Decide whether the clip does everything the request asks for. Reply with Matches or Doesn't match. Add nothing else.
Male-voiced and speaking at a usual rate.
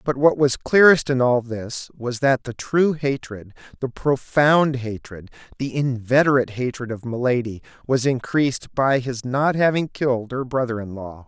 Matches